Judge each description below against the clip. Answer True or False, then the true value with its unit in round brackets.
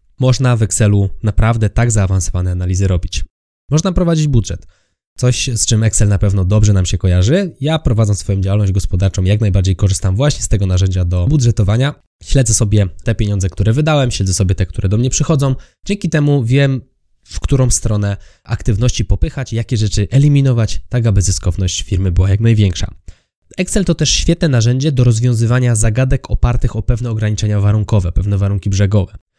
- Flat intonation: False (4.5 semitones)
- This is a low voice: True (110 Hz)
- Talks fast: True (165 wpm)